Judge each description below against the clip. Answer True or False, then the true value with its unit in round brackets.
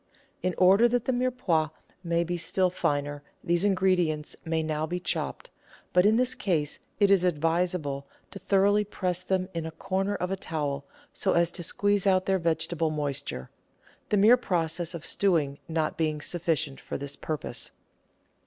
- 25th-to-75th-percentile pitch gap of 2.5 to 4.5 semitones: True (3.6 semitones)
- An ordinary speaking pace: True (170 wpm)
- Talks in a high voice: False (175 Hz)